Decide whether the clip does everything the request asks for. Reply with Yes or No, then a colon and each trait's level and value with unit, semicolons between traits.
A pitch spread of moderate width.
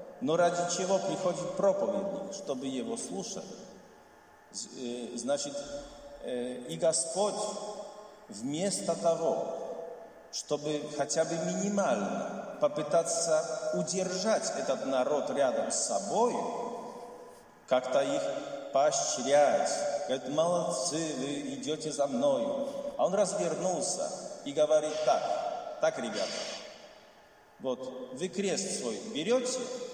No: wide, 7.4 semitones